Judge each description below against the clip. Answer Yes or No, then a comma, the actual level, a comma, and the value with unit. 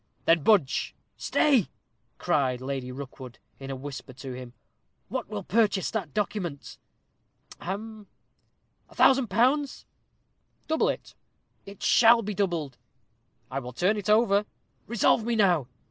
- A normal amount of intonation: No, wide, 8.2 semitones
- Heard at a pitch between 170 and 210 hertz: Yes, high, 190 Hz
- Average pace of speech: No, slow, 130 wpm